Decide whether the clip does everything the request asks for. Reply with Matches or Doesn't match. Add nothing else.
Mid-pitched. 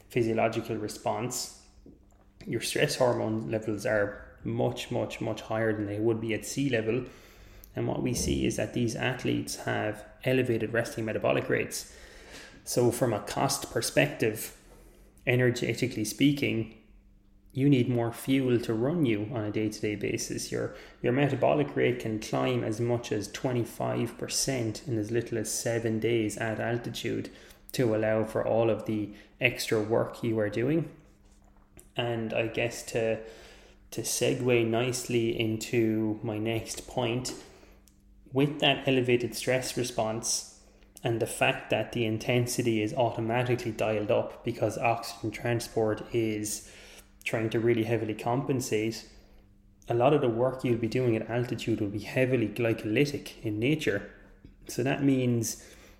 Doesn't match